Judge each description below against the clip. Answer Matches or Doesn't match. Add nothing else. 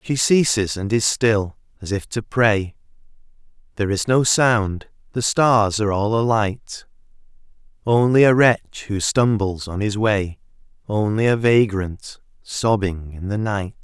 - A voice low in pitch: Matches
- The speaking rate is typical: Matches